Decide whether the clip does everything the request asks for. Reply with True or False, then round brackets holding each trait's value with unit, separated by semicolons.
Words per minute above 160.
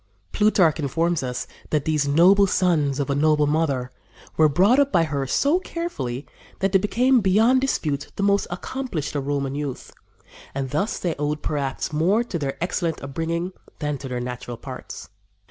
True (170 wpm)